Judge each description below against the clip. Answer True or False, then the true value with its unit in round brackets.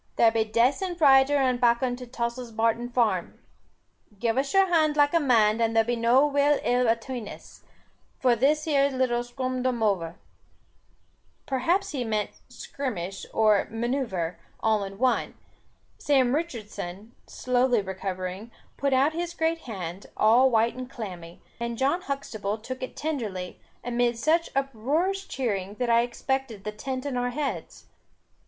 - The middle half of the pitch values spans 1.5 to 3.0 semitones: False (3.8 semitones)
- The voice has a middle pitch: False (245 Hz)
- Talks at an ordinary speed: True (145 wpm)